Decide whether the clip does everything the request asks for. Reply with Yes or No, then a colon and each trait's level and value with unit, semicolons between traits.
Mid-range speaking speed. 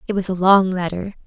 No: fast, 235 wpm